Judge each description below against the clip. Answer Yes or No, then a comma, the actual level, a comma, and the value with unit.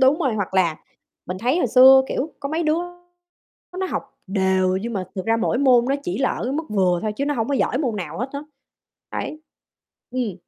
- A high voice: Yes, high, 245 Hz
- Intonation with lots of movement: Yes, wide, 6.3 semitones